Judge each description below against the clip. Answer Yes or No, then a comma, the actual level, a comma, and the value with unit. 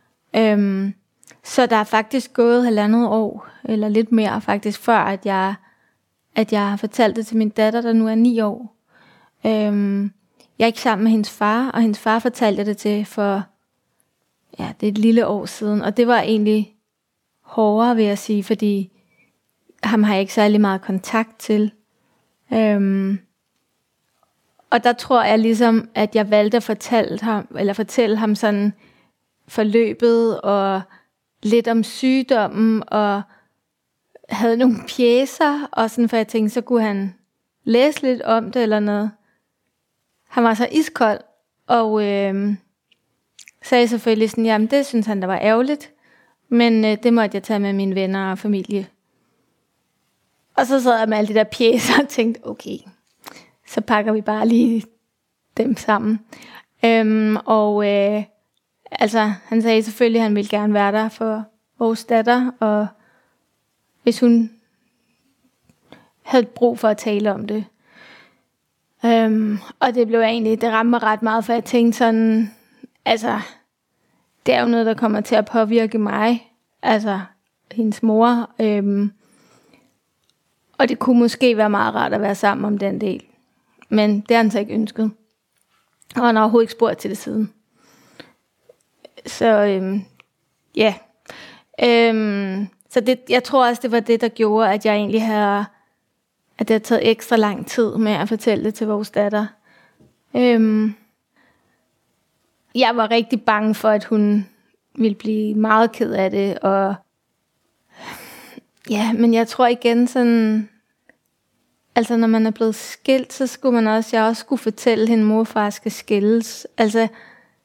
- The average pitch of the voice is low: No, high, 220 Hz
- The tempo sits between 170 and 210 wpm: No, average, 160 wpm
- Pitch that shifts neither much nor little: No, narrow, 1.9 semitones